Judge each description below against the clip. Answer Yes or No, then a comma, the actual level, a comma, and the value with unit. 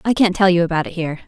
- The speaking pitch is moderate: Yes, medium, 180 Hz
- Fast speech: Yes, fast, 330 wpm